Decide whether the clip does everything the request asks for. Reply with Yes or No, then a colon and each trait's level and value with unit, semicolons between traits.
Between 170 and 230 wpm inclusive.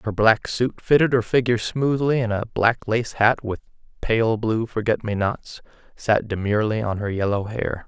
Yes: average, 185 wpm